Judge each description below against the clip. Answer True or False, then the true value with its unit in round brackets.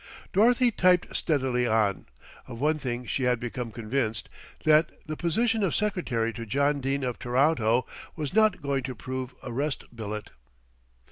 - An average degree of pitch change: True (4.6 semitones)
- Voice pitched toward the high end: False (130 Hz)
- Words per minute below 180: True (155 wpm)